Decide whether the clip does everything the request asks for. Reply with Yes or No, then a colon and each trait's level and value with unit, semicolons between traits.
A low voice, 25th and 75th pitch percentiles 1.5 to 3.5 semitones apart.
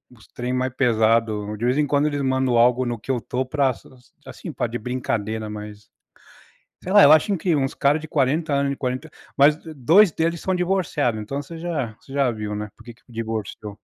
No: low, 130 Hz; average, 4.5 semitones